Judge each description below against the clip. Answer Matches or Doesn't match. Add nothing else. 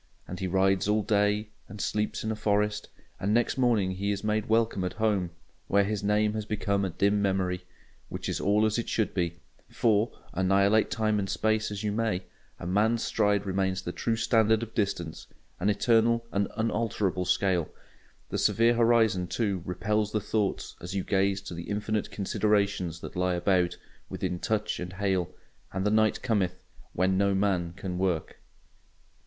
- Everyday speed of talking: Matches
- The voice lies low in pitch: Matches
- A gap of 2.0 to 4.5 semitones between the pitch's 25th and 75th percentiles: Matches